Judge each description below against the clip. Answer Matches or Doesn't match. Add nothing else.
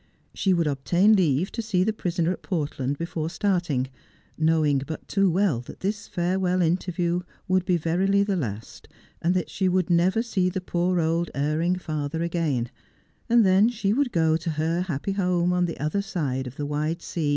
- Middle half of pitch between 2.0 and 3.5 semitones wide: Matches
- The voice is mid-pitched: Matches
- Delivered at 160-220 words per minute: Matches